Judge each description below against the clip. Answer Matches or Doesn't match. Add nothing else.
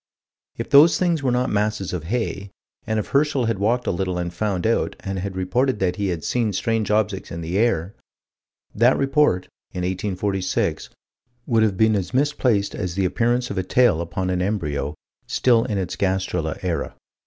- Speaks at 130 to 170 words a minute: Doesn't match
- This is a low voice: Matches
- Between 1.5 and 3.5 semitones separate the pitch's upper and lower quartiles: Doesn't match